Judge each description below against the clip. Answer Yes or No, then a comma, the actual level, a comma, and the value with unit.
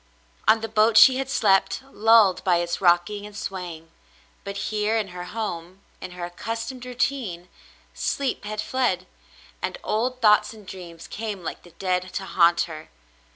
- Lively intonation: No, average, 3.9 semitones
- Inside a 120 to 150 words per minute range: No, average, 170 wpm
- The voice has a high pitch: Yes, high, 200 Hz